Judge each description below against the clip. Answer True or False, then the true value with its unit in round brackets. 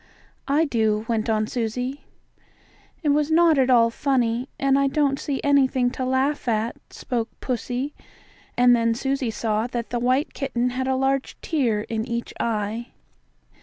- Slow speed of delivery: False (160 wpm)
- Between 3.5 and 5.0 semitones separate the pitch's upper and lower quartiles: False (3.0 semitones)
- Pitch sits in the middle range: False (250 Hz)